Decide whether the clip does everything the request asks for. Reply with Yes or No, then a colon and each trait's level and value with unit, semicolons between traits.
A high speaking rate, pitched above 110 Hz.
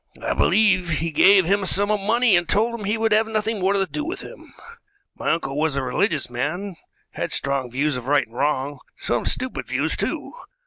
Yes: fast, 215 wpm; medium, 185 Hz